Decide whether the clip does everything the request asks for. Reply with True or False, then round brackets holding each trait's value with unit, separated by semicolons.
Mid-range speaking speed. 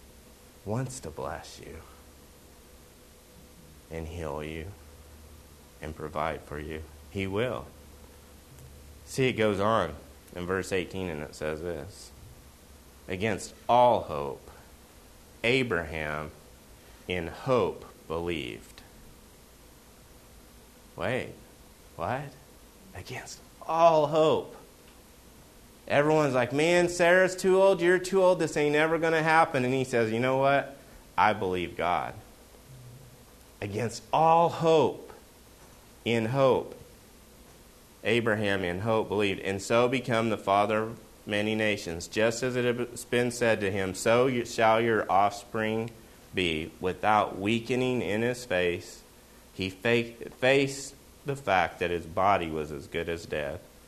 False (120 wpm)